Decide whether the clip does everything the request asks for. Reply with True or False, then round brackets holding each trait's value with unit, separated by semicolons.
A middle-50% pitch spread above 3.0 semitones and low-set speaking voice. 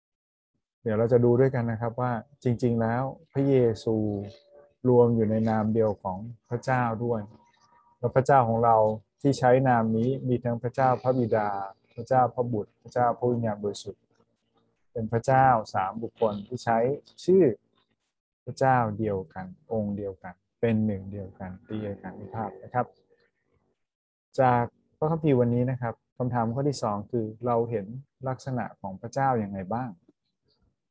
False (2.7 semitones; 115 Hz)